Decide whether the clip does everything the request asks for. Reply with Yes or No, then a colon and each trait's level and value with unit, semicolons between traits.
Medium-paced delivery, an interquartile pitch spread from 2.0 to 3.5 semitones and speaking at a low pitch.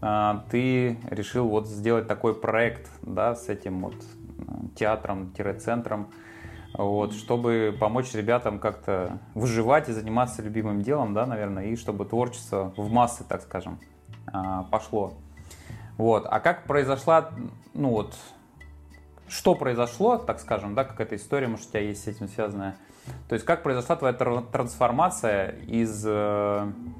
Yes: average, 130 wpm; average, 3.0 semitones; low, 110 Hz